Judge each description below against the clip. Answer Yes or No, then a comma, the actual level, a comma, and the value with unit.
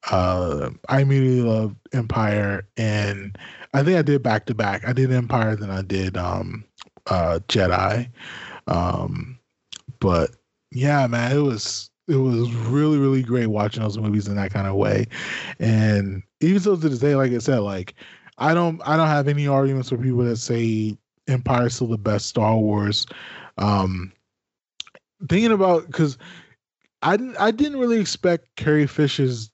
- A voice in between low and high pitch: No, low, 120 Hz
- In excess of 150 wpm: Yes, average, 165 wpm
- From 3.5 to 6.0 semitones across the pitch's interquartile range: Yes, wide, 5.6 semitones